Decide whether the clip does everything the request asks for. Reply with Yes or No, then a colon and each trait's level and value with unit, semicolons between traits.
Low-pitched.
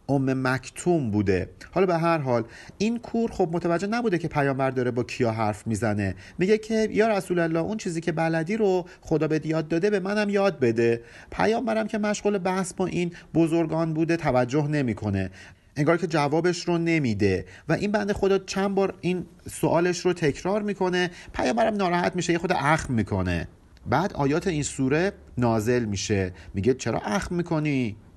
No: medium, 165 Hz